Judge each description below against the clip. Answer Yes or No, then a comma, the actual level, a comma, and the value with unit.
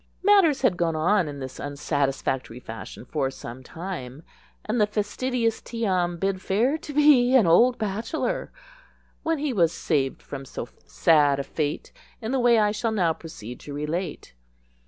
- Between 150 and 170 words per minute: Yes, average, 165 wpm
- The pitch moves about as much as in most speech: No, wide, 8.5 semitones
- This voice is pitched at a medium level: Yes, medium, 180 Hz